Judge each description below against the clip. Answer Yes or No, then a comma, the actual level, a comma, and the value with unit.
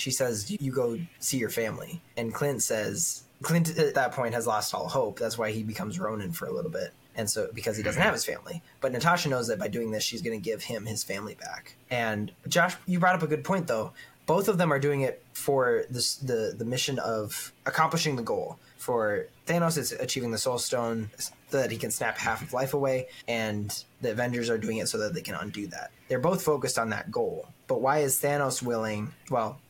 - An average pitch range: No, wide, 6.4 semitones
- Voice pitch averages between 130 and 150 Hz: Yes, low, 135 Hz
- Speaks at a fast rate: Yes, fast, 230 wpm